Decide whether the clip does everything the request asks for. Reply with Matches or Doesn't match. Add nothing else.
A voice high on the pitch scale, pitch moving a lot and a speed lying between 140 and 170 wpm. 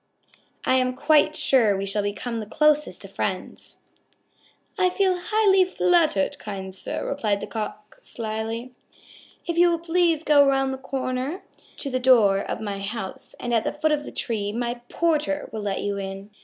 Matches